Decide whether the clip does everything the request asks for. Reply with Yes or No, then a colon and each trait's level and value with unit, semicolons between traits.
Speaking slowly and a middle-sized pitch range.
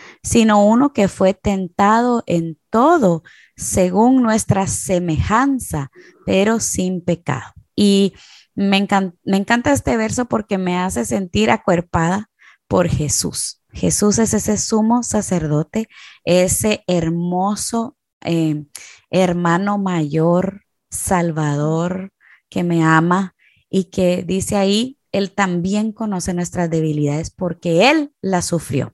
Yes: slow, 110 wpm; average, 3.7 semitones